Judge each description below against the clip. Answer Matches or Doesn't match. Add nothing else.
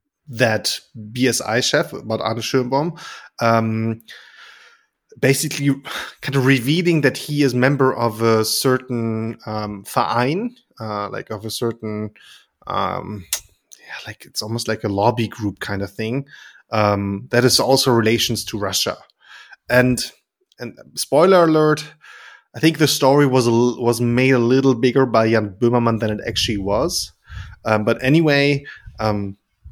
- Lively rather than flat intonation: Doesn't match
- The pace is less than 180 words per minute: Matches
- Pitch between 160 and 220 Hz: Doesn't match